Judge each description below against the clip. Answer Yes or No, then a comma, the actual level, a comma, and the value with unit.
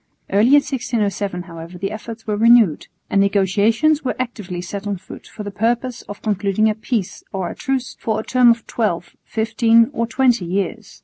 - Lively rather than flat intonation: No, average, 3.1 semitones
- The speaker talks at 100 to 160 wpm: No, average, 185 wpm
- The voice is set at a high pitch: Yes, high, 215 Hz